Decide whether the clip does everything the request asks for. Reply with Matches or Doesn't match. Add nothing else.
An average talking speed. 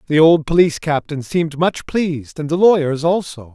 Matches